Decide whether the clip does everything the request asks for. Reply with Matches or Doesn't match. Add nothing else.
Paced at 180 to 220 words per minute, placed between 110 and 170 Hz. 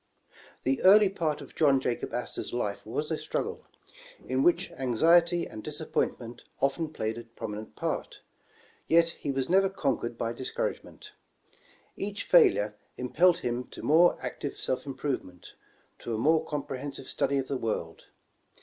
Doesn't match